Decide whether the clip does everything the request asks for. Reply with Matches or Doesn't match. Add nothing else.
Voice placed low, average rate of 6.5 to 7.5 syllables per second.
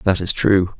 Doesn't match